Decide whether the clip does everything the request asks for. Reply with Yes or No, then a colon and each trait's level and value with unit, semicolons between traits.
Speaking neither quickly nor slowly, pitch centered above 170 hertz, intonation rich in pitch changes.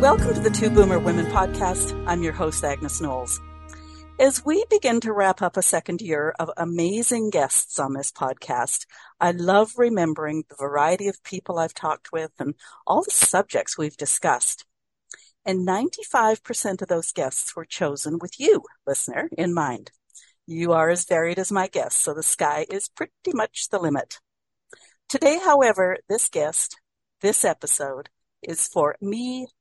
Yes: average, 160 wpm; medium, 185 Hz; wide, 6.4 semitones